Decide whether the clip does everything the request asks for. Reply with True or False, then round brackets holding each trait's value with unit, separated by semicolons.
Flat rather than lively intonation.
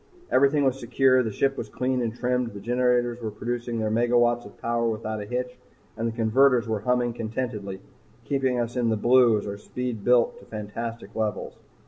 True (2.2 semitones)